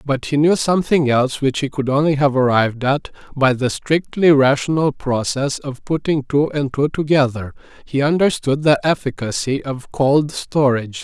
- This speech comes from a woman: No, male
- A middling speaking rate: Yes, average, 160 wpm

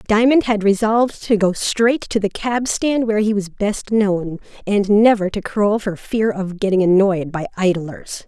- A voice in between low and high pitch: No, high, 205 Hz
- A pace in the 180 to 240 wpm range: Yes, average, 190 wpm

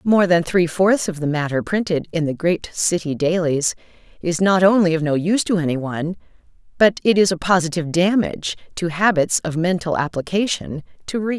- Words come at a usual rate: Yes, average, 185 wpm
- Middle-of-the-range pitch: Yes, medium, 170 Hz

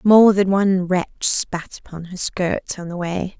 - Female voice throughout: Yes, female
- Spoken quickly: No, average, 195 wpm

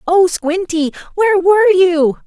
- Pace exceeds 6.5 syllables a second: Yes, 7.1 syllables/s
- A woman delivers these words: Yes, female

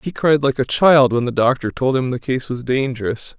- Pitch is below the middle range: Yes, low, 130 Hz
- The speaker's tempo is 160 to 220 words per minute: No, fast, 250 wpm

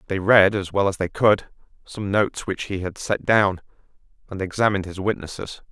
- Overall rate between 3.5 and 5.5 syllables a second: Yes, 5.4 syllables/s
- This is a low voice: Yes, very low, 95 Hz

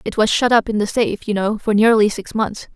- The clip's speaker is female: Yes, female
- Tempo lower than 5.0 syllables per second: No, 5.7 syllables/s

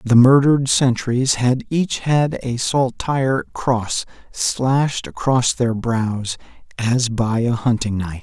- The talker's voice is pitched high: No, low, 125 Hz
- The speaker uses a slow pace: Yes, slow, 130 wpm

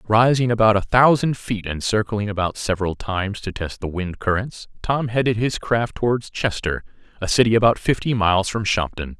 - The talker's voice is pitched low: Yes, low, 105 Hz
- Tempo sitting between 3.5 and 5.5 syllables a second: Yes, 5.3 syllables/s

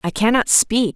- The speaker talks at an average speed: Yes, average, 190 wpm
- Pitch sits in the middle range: No, high, 220 Hz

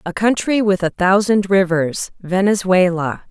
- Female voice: Yes, female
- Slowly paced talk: Yes, slow, 110 wpm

